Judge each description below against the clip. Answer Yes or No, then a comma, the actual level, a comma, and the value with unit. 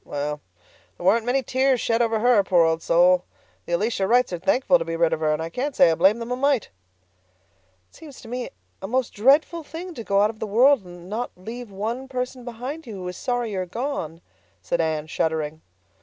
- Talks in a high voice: Yes, high, 220 Hz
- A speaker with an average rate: No, fast, 225 wpm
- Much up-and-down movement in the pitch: Yes, wide, 6.3 semitones